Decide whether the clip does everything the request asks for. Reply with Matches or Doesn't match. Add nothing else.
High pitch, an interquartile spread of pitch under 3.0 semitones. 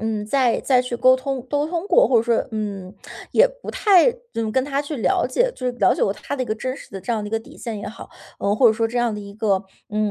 Doesn't match